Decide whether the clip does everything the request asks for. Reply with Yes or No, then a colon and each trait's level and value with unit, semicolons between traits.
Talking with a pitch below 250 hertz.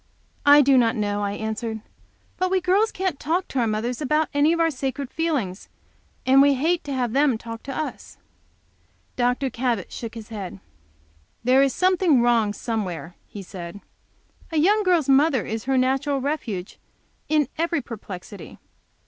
No: very high, 260 Hz